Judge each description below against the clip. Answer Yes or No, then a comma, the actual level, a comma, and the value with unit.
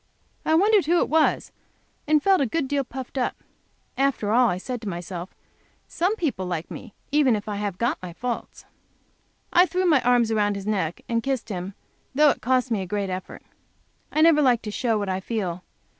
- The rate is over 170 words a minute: Yes, average, 200 wpm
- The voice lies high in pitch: Yes, high, 235 Hz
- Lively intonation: Yes, wide, 6.4 semitones